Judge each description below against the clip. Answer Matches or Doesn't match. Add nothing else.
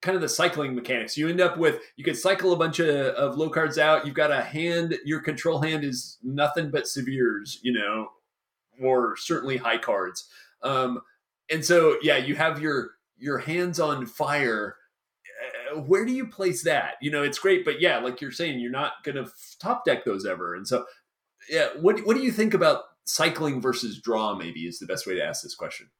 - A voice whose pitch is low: Doesn't match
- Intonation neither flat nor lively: Matches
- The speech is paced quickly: Matches